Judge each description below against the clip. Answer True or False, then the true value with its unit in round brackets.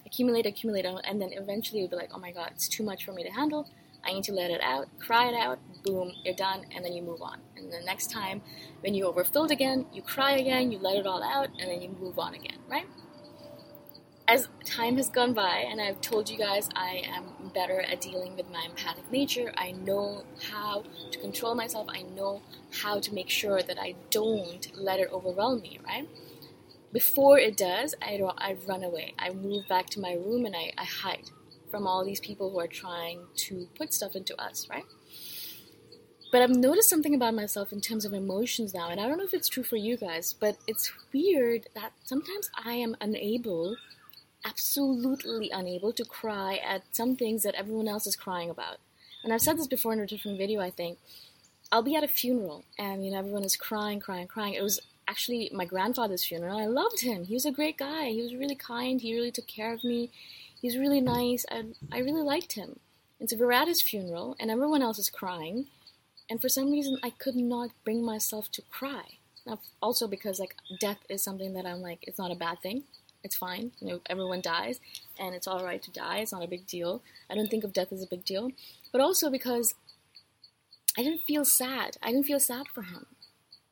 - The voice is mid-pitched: False (210 Hz)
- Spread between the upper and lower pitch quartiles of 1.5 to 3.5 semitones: False (4.8 semitones)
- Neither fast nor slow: False (215 wpm)